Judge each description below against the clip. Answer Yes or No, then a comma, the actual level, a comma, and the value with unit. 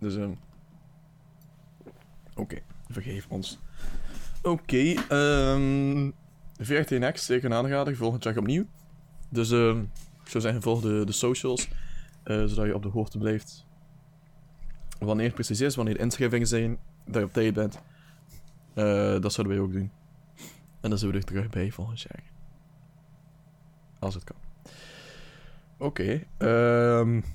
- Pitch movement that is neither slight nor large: No, wide, 6.0 semitones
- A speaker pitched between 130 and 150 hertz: Yes, medium, 140 Hz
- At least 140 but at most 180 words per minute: Yes, average, 155 wpm